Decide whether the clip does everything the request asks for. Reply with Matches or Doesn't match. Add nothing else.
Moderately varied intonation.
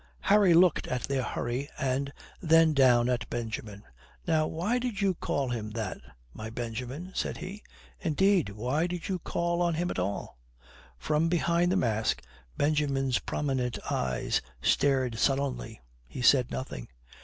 Doesn't match